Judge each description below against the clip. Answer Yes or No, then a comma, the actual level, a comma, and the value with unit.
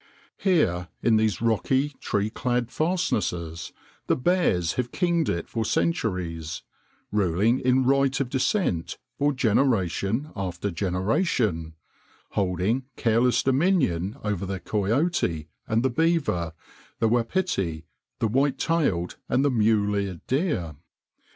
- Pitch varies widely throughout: Yes, wide, 6.9 semitones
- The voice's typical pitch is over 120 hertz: No, low, 115 Hz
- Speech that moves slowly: Yes, slow, 120 wpm